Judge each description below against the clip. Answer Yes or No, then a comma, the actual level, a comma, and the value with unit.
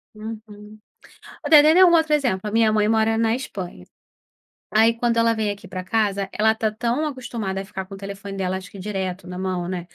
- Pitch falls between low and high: No, high, 215 Hz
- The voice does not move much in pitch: No, average, 3.1 semitones